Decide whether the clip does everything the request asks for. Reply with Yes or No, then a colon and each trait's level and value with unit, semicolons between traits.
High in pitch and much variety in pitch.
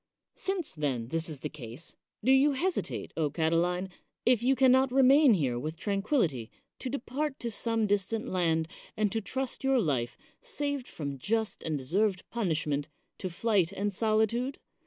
Yes: high, 205 Hz; wide, 8.1 semitones